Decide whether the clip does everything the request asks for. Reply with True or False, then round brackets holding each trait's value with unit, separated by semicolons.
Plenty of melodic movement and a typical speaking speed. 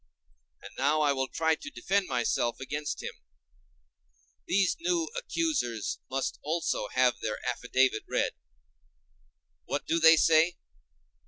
False (5.7 semitones; 120 wpm)